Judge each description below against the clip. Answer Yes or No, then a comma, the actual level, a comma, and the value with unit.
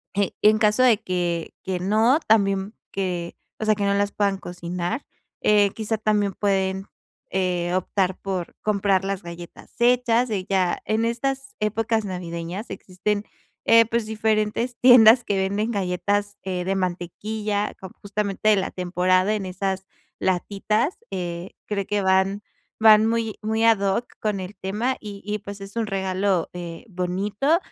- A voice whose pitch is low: No, high, 200 Hz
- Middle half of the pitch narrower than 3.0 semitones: Yes, narrow, 2.6 semitones